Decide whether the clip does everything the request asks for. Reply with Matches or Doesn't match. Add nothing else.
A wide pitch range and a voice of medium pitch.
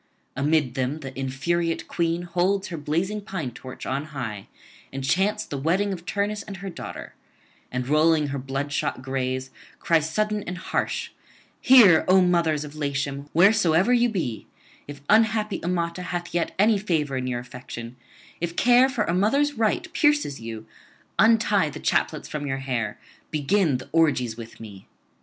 Matches